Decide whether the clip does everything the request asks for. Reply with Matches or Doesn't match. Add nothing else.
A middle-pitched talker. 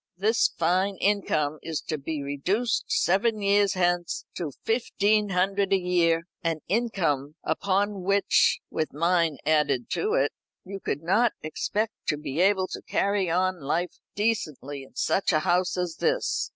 Matches